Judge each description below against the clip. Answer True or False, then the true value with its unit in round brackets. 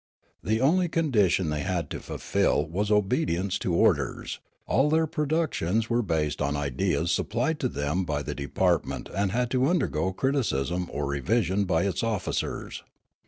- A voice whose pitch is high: False (95 Hz)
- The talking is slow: False (170 wpm)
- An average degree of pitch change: False (7.1 semitones)